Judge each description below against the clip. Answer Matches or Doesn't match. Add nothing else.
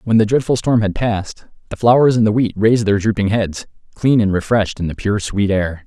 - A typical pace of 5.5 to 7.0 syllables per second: Matches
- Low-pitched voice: Matches